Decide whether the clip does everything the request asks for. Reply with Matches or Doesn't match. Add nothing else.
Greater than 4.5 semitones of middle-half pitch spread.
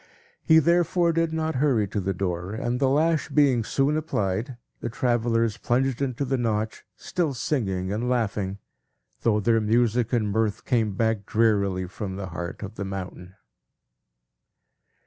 Matches